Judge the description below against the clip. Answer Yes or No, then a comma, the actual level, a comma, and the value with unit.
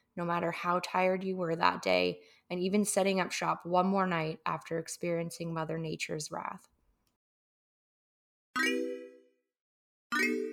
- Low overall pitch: No, medium, 165 Hz